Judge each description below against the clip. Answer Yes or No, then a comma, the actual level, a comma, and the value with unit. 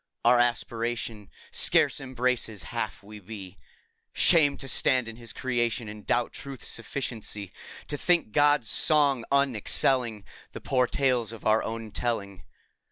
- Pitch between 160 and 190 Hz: No, low, 120 Hz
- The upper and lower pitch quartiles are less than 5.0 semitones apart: Yes, average, 3.4 semitones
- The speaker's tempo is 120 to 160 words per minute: Yes, slow, 135 wpm